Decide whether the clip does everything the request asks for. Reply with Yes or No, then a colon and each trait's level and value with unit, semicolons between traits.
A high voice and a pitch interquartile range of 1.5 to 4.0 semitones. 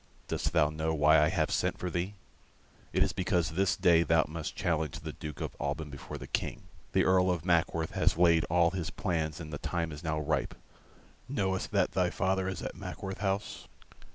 No: very low, 85 Hz; average, 2.9 semitones